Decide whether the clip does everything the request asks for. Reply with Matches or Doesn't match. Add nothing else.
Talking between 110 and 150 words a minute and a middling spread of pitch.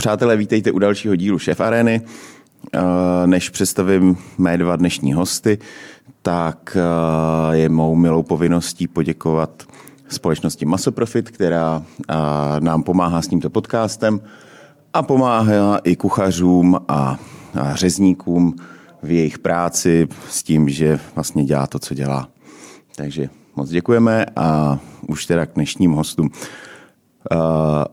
Matches